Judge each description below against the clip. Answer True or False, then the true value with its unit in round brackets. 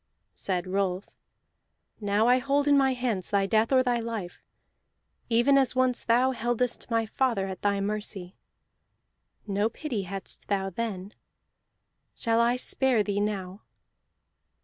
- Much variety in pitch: False (4.0 semitones)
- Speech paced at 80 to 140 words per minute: True (135 wpm)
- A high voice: True (220 Hz)